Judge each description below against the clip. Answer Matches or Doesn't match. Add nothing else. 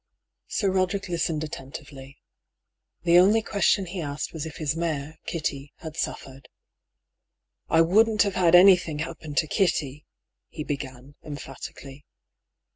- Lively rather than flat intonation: Doesn't match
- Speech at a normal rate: Doesn't match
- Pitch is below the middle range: Doesn't match